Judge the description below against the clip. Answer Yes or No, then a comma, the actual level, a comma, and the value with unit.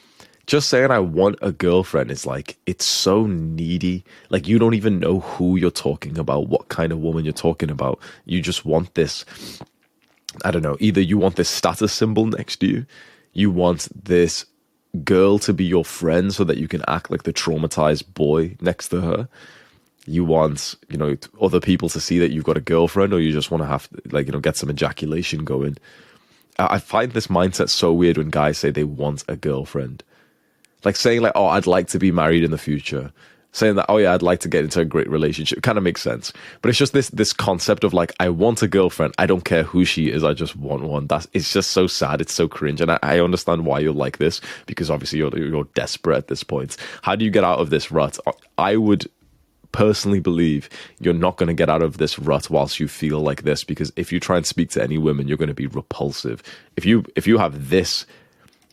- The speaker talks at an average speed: No, fast, 225 wpm